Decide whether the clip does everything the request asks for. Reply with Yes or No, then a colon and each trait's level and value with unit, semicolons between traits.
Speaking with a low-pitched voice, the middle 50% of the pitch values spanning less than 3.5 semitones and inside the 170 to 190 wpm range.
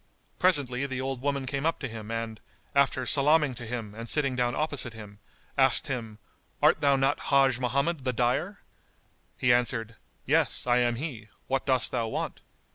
Yes: low, 130 Hz; average, 2.8 semitones; average, 175 wpm